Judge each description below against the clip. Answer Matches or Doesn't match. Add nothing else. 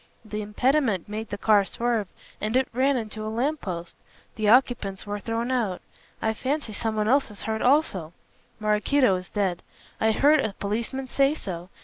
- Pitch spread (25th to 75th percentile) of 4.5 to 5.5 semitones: Doesn't match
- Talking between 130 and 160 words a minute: Doesn't match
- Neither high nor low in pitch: Doesn't match